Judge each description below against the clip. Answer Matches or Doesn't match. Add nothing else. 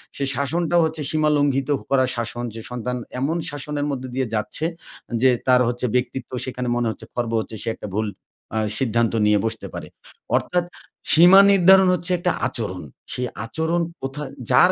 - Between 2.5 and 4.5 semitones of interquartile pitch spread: Doesn't match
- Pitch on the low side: Matches